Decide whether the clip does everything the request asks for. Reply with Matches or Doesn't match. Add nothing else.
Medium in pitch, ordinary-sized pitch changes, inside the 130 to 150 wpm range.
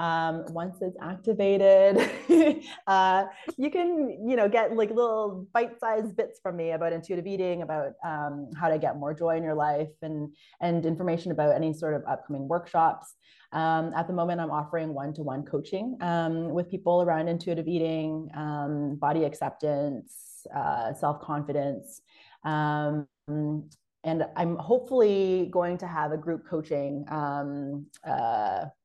Matches